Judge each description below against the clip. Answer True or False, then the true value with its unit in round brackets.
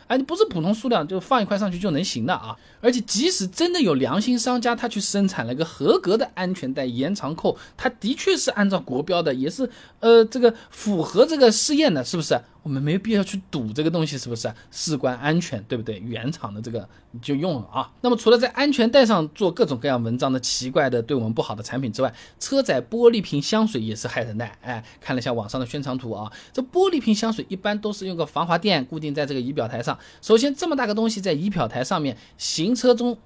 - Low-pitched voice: False (185 Hz)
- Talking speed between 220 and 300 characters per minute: False (355 characters per minute)